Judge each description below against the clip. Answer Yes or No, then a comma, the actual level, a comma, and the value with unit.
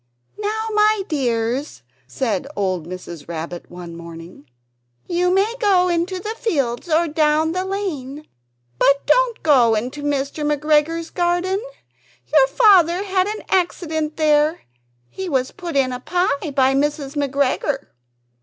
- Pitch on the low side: No, very high, 300 Hz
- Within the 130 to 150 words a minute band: Yes, slow, 135 wpm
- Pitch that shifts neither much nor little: No, wide, 5.8 semitones